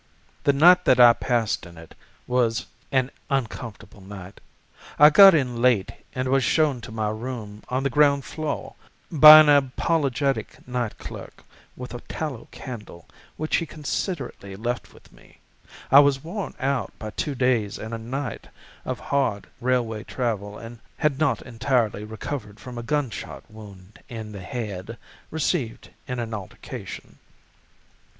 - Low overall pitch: Yes, low, 125 Hz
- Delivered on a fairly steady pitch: No, average, 4.3 semitones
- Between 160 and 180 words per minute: No, average, 150 wpm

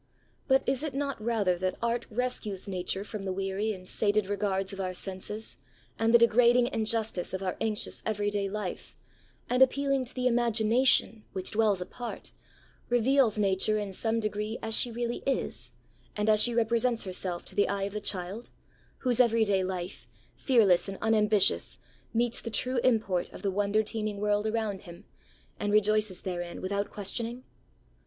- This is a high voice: Yes, high, 215 Hz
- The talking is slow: No, average, 165 wpm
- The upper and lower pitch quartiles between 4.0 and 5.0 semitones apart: No, average, 3.2 semitones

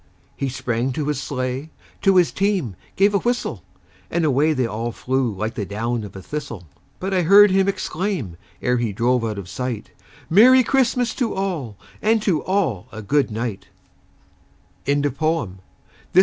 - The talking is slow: No, average, 160 wpm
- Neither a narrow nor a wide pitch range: No, wide, 8.9 semitones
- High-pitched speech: No, low, 135 Hz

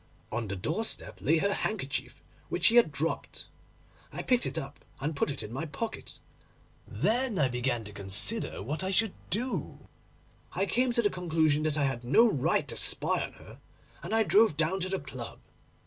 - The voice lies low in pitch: No, medium, 155 Hz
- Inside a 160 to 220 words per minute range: Yes, average, 190 wpm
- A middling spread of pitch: No, wide, 7.7 semitones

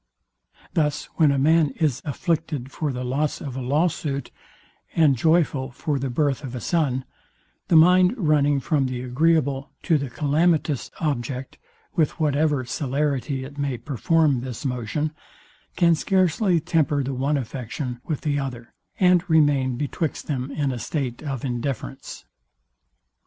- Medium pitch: Yes, medium, 145 Hz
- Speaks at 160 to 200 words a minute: No, average, 145 wpm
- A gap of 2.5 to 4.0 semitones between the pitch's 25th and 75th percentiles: Yes, average, 3.3 semitones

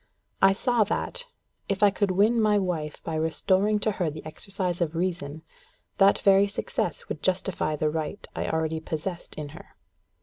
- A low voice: No, medium, 185 Hz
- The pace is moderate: Yes, average, 170 wpm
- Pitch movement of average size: Yes, average, 4.0 semitones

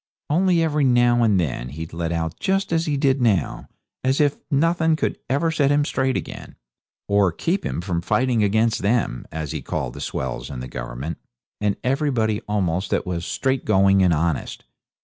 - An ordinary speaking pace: Yes, average, 180 wpm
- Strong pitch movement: Yes, wide, 8.9 semitones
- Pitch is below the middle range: Yes, low, 110 Hz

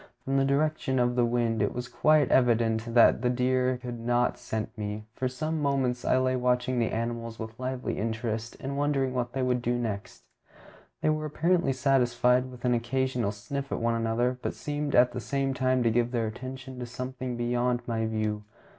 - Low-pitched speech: Yes, low, 125 Hz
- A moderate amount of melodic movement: No, narrow, 2.0 semitones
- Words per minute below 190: No, average, 200 wpm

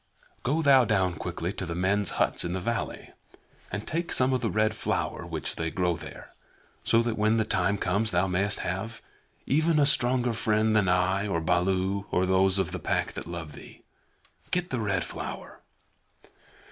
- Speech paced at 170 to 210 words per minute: Yes, average, 185 wpm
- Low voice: Yes, low, 100 Hz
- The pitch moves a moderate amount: Yes, average, 4.0 semitones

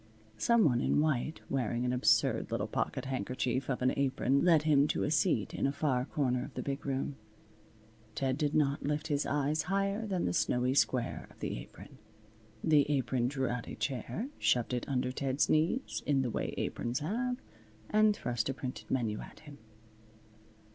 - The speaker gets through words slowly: No, average, 180 wpm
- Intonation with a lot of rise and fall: No, average, 3.3 semitones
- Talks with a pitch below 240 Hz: Yes, low, 135 Hz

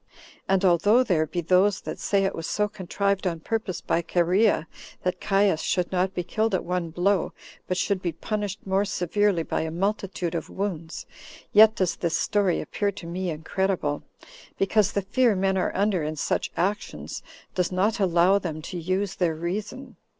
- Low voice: No, medium, 185 Hz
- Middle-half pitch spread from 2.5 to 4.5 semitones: Yes, average, 2.8 semitones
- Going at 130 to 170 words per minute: No, average, 180 wpm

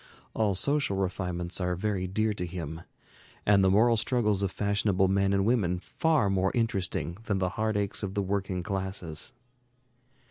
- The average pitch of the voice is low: Yes, low, 100 Hz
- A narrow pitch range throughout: Yes, narrow, 2.3 semitones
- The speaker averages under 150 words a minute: No, average, 165 wpm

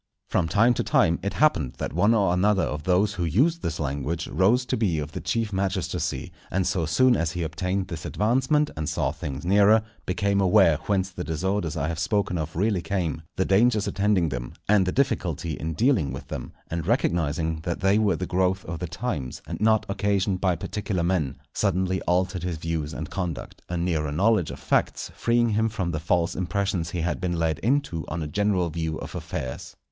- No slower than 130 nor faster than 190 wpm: No, fast, 205 wpm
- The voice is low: Yes, very low, 90 Hz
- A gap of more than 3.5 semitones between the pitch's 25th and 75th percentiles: Yes, average, 3.9 semitones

